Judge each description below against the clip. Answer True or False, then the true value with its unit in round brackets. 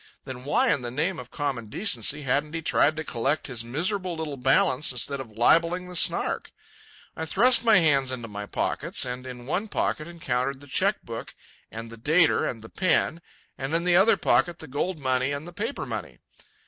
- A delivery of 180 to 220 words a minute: True (200 wpm)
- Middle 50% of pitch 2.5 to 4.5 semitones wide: False (5.2 semitones)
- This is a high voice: False (145 Hz)